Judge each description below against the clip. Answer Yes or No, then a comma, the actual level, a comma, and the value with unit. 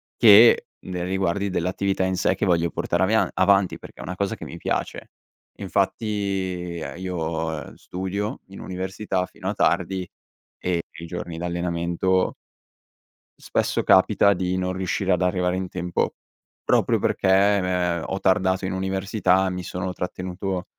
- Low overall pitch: Yes, very low, 95 Hz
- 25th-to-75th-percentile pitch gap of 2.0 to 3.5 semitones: No, narrow, 1.2 semitones